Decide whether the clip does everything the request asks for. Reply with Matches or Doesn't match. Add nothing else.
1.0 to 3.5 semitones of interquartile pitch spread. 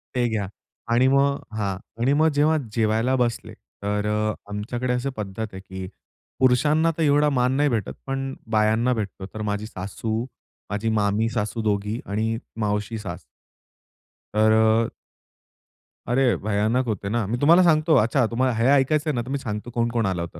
Doesn't match